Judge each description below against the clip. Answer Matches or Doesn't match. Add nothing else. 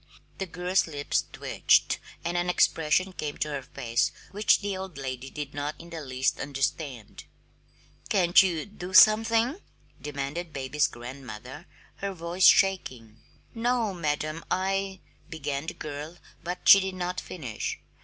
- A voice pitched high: Doesn't match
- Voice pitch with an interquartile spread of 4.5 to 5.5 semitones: Matches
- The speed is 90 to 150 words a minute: Matches